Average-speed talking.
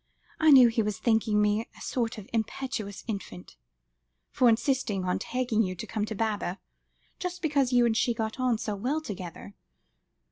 Yes: average, 175 wpm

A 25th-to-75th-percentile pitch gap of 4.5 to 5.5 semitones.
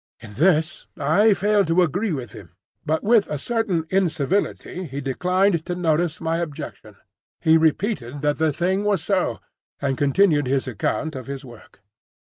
Yes: average, 5.1 semitones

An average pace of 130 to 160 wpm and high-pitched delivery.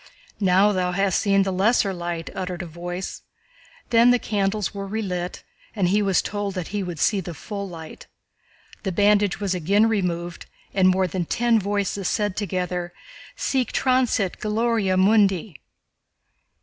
Yes: average, 150 wpm; high, 195 Hz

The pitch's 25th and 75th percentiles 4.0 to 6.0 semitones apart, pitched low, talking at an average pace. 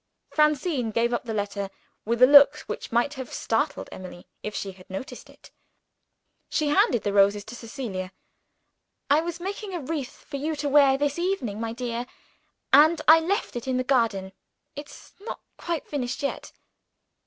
No: average, 5.2 semitones; very high, 260 Hz; average, 170 wpm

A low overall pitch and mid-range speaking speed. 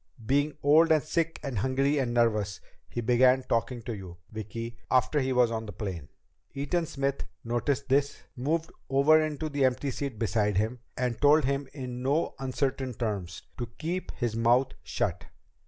Yes: low, 130 Hz; average, 170 wpm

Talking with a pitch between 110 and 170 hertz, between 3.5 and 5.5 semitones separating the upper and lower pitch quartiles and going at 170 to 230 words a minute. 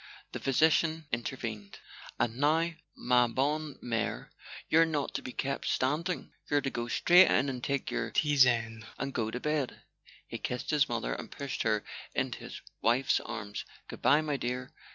Yes: low, 135 Hz; average, 4.1 semitones; average, 175 wpm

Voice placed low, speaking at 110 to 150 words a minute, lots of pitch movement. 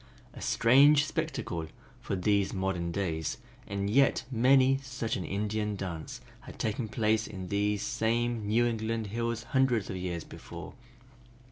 No: low, 110 Hz; average, 140 wpm; average, 3.6 semitones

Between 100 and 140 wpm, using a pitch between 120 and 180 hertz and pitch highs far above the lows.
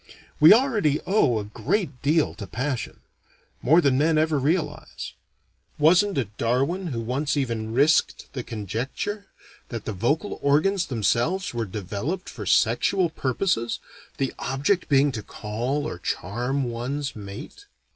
Yes: slow, 135 wpm; medium, 140 Hz; wide, 5.7 semitones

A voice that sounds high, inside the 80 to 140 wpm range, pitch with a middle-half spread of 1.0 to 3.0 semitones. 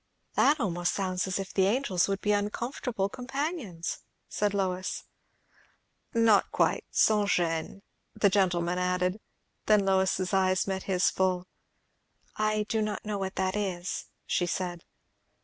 Yes: high, 195 Hz; slow, 135 wpm; narrow, 2.5 semitones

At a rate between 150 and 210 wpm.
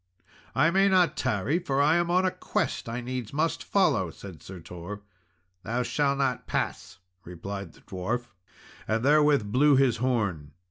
Yes: average, 165 wpm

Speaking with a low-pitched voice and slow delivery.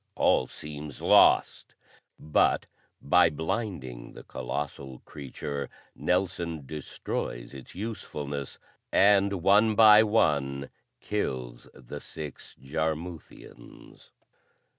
Yes: very low, 75 Hz; slow, 85 wpm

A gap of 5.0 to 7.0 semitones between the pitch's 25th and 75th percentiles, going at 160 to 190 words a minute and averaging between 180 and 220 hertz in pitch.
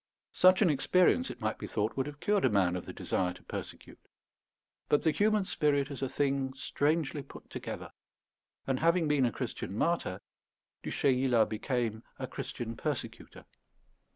No: average, 5.3 semitones; average, 165 wpm; low, 135 Hz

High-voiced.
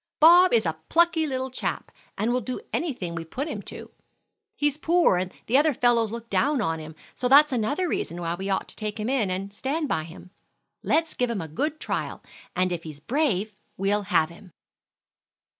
Yes: high, 230 Hz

